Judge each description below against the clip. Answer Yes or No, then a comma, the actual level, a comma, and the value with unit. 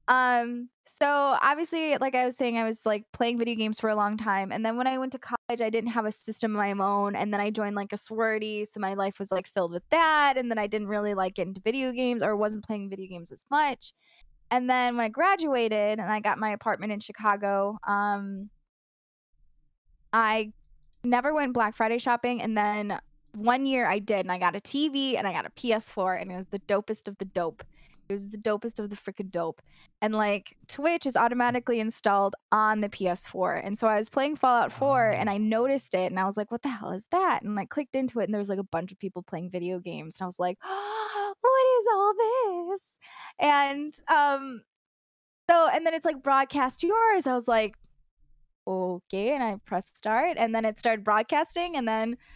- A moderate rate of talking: No, fast, 225 wpm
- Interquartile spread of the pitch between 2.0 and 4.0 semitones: No, average, 4.4 semitones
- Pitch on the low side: No, high, 220 Hz